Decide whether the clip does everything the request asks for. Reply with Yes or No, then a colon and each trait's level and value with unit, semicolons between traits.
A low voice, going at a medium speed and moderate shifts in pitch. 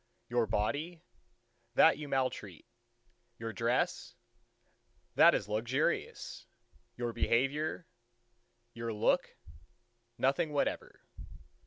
No: low, 120 Hz; slow, 75 wpm; average, 3.9 semitones